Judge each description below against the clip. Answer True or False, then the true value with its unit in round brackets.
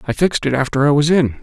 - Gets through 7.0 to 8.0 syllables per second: True (7.4 syllables/s)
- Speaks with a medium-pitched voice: True (145 Hz)